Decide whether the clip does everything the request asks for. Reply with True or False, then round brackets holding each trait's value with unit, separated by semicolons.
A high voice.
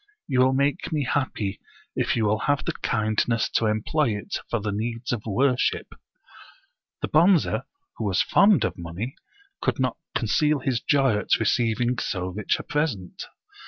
False (120 Hz)